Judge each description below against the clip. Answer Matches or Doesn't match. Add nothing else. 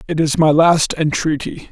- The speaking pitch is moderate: Matches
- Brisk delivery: Doesn't match